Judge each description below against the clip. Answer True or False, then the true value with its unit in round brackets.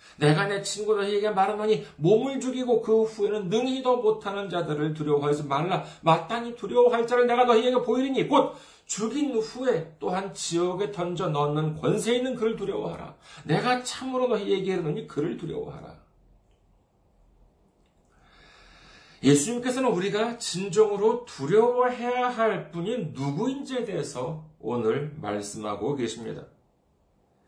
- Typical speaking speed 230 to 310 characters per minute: True (305 characters per minute)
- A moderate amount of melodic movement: False (7.5 semitones)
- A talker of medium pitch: False (205 Hz)